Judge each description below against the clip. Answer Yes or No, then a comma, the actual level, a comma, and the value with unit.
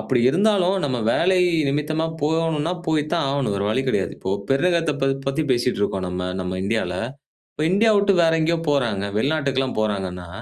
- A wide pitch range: Yes, wide, 7.7 semitones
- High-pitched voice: No, medium, 140 Hz